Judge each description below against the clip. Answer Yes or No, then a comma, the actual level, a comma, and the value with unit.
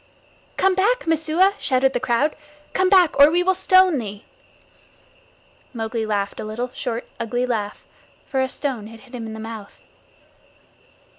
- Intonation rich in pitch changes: Yes, wide, 6.7 semitones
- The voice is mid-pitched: No, very high, 255 Hz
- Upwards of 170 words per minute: No, average, 155 wpm